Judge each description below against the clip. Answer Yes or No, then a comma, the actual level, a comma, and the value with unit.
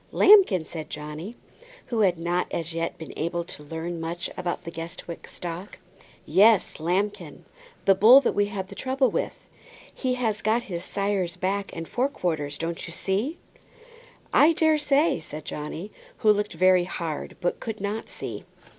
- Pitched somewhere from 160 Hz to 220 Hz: Yes, medium, 185 Hz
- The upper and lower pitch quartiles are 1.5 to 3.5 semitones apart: No, average, 4.5 semitones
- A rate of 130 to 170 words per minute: Yes, average, 165 wpm